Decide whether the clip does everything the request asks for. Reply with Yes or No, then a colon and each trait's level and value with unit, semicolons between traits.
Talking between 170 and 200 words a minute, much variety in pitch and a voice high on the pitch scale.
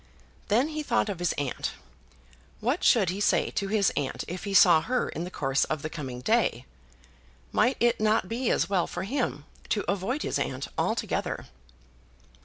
Yes: average, 180 wpm; wide, 7.0 semitones; high, 200 Hz